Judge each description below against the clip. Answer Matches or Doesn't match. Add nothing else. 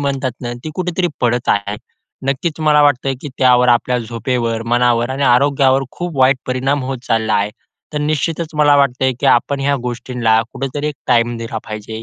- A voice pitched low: Matches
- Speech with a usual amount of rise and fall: Matches